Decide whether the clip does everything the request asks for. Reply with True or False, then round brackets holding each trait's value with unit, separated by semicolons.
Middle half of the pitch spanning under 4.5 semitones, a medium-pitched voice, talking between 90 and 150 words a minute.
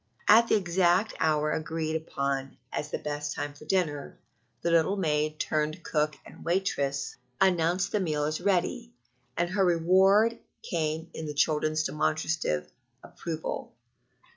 True (3.3 semitones; 160 Hz; 140 wpm)